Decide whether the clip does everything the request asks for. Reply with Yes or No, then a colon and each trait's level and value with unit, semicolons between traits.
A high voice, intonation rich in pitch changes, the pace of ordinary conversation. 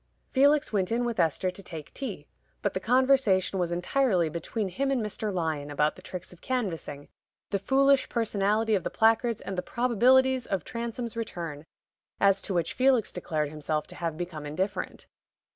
Yes: high, 200 Hz; wide, 6.1 semitones; average, 175 wpm